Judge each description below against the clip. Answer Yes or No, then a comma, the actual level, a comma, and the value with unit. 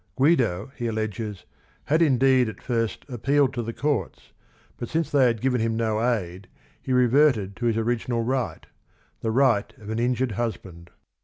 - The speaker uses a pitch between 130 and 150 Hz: No, low, 120 Hz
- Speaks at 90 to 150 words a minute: No, average, 170 wpm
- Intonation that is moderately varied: Yes, average, 3.1 semitones